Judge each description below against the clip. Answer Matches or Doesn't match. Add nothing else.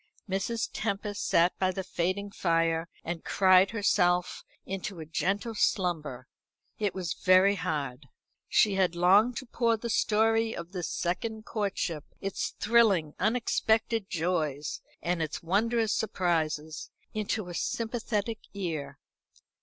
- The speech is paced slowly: Matches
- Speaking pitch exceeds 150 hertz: Matches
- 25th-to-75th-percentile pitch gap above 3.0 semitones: Matches